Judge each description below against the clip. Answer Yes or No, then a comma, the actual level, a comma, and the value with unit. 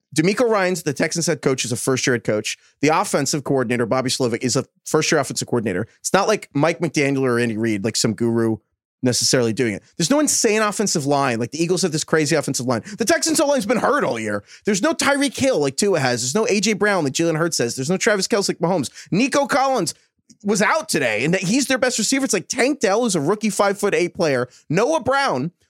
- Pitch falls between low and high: Yes, medium, 170 Hz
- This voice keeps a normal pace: No, fast, 240 wpm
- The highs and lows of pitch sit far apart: Yes, wide, 8.8 semitones